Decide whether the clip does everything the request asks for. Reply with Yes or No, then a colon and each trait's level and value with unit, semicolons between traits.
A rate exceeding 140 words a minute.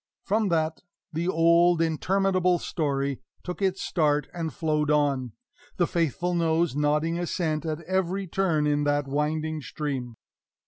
No: slow, 135 wpm